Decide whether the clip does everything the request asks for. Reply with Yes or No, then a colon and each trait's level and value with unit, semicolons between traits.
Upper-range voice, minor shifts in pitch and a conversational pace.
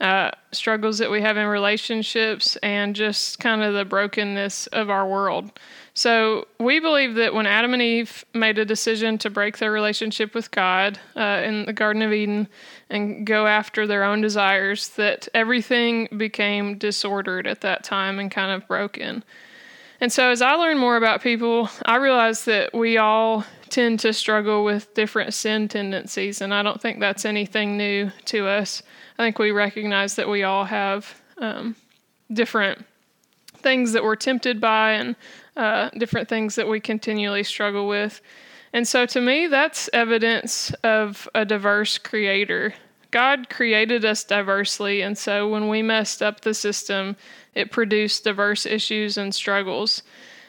Yes: high, 215 Hz; narrow, 2.1 semitones; average, 165 wpm